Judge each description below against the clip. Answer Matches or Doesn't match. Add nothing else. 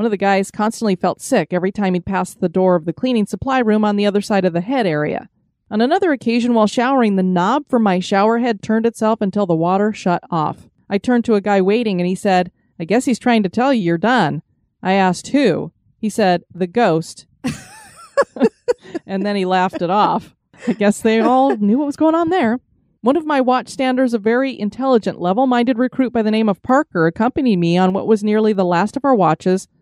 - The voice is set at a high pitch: Matches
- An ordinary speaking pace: Doesn't match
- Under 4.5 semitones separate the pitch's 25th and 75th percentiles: Doesn't match